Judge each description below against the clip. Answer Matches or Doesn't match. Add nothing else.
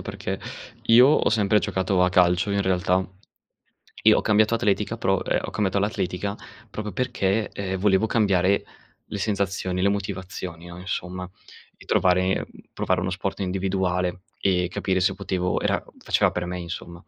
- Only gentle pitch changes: Matches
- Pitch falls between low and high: Doesn't match